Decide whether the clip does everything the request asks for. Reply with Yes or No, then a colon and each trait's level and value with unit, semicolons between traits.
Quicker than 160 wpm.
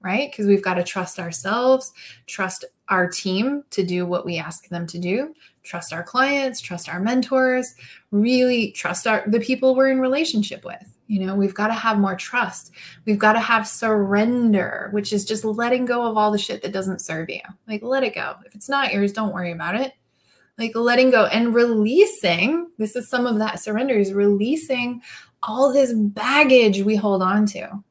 Yes: average, 195 wpm